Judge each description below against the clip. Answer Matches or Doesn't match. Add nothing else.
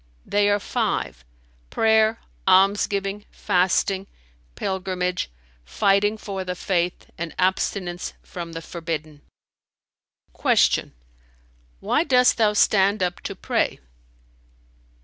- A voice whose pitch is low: Doesn't match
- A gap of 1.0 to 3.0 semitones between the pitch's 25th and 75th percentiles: Matches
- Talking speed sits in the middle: Doesn't match